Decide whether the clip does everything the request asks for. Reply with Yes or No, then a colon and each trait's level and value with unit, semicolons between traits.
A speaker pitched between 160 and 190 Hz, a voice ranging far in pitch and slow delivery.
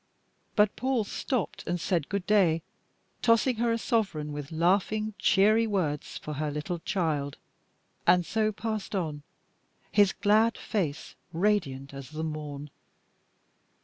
Yes: medium, 185 Hz; wide, 5.9 semitones; slow, 130 wpm